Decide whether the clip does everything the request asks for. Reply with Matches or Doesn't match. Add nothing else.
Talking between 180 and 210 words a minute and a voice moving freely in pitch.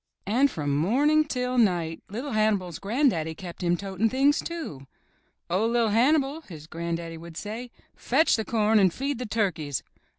Doesn't match